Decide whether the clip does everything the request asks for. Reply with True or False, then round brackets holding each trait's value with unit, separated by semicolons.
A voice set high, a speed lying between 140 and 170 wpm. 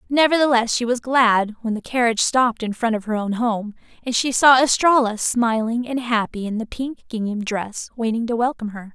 False (235 Hz; 200 wpm)